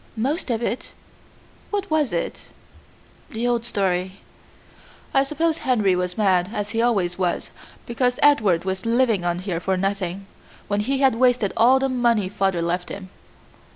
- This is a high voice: Yes, high, 210 Hz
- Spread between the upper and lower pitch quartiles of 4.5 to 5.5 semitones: Yes, average, 5.0 semitones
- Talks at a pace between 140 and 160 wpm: Yes, average, 155 wpm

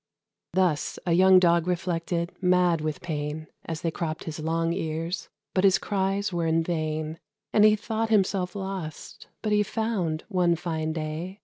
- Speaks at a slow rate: No, average, 165 wpm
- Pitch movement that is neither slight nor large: Yes, average, 3.0 semitones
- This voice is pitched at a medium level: Yes, medium, 175 Hz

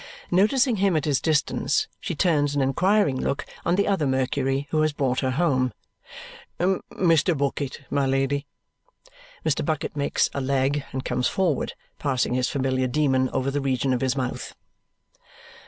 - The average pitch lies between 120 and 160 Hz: Yes, medium, 140 Hz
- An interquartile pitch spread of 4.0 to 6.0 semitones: No, average, 3.2 semitones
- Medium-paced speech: Yes, average, 155 wpm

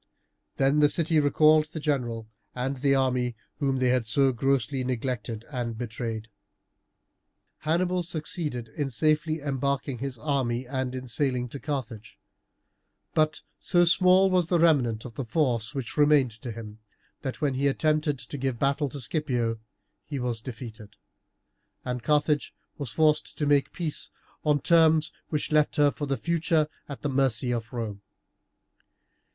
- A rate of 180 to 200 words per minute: No, average, 150 wpm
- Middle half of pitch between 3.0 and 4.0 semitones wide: Yes, average, 3.7 semitones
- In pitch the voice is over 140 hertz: No, low, 135 Hz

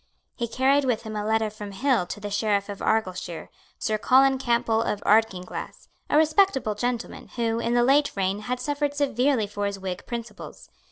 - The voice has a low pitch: No, high, 225 Hz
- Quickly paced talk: No, average, 180 wpm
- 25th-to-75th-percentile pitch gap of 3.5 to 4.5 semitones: Yes, average, 4.1 semitones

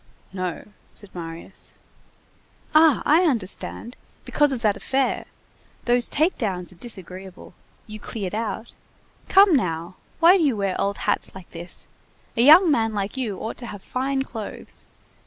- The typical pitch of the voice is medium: No, high, 225 Hz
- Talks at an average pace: Yes, average, 150 wpm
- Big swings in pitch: Yes, wide, 6.1 semitones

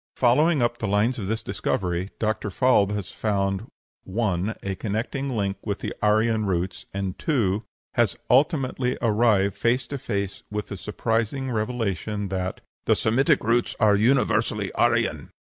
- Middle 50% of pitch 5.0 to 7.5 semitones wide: No, average, 3.6 semitones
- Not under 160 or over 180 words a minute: No, average, 145 wpm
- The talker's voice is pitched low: Yes, low, 110 Hz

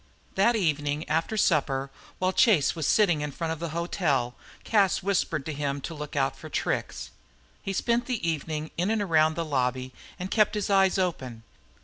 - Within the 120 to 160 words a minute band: No, average, 180 wpm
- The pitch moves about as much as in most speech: Yes, average, 4.8 semitones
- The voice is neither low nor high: Yes, medium, 165 Hz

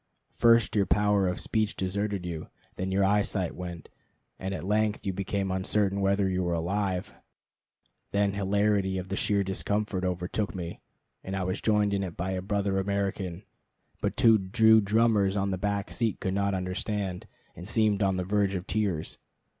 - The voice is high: No, low, 100 Hz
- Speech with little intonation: Yes, narrow, 1.8 semitones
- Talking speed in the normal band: Yes, average, 175 wpm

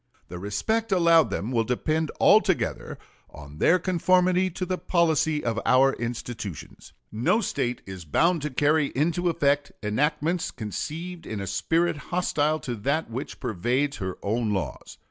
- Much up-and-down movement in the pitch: Yes, wide, 7.0 semitones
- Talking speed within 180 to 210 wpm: No, average, 145 wpm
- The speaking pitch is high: No, medium, 145 Hz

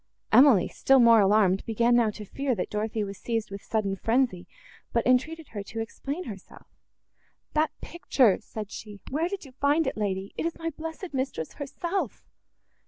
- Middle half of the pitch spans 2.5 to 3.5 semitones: No, wide, 5.5 semitones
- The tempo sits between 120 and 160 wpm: No, average, 170 wpm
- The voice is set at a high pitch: Yes, high, 235 Hz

